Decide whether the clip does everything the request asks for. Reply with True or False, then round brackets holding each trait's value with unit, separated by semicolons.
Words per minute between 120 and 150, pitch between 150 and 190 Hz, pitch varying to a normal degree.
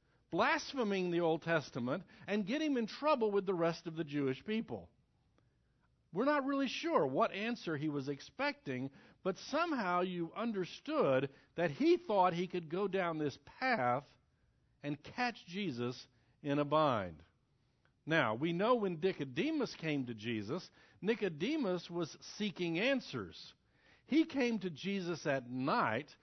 False (140 wpm; 180 Hz; 7.7 semitones)